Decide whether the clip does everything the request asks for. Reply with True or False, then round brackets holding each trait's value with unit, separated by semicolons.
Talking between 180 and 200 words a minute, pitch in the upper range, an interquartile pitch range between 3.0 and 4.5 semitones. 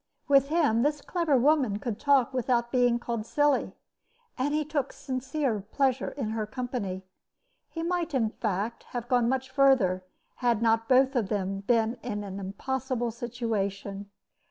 False (155 wpm; 245 Hz; 3.9 semitones)